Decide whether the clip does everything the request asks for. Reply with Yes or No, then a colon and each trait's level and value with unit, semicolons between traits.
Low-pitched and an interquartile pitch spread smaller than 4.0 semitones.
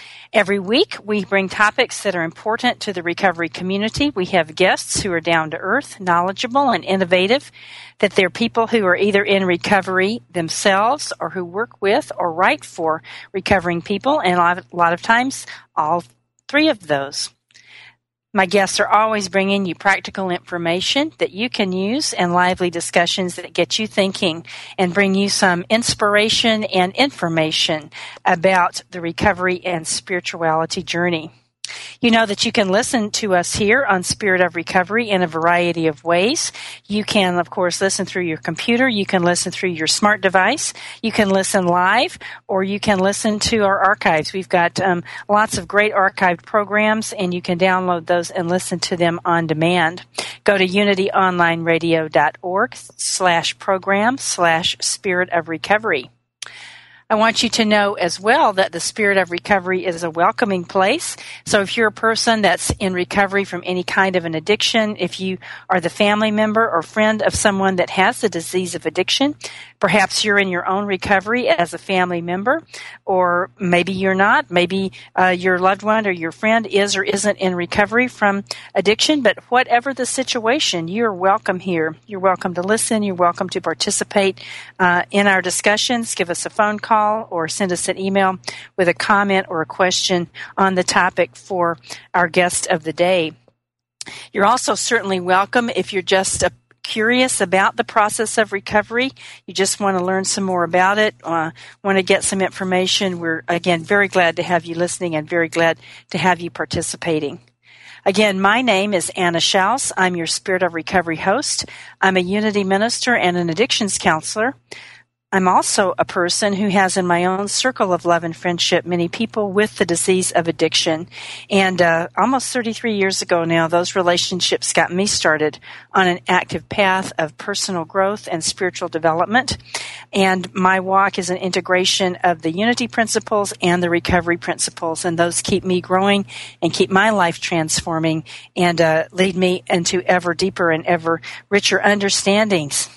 No: high, 190 Hz; average, 2.9 semitones